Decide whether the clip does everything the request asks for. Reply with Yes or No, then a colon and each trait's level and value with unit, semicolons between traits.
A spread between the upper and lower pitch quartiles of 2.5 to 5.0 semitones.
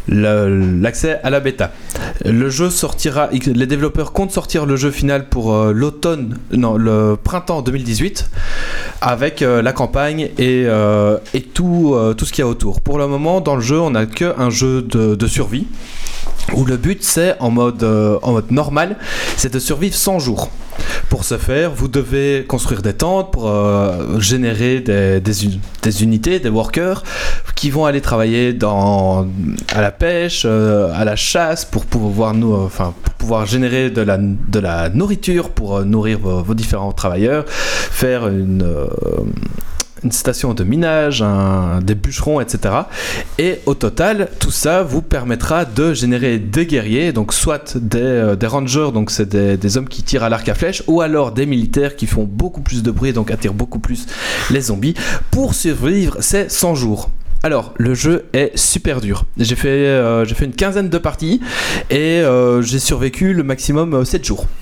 No: wide, 5.4 semitones